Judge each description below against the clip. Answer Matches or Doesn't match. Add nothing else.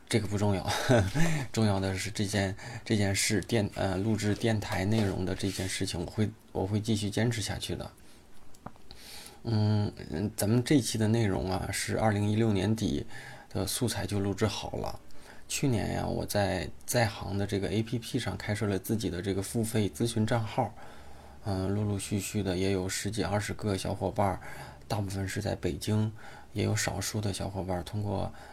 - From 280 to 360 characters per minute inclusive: Doesn't match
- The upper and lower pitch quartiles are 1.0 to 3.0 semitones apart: Matches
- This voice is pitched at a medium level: Doesn't match